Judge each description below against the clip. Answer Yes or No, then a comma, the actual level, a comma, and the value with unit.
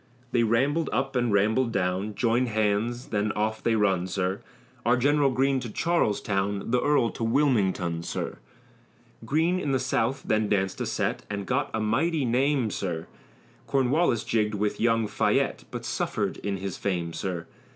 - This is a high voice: No, low, 115 Hz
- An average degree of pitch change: Yes, average, 4.5 semitones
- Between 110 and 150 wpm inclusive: No, average, 160 wpm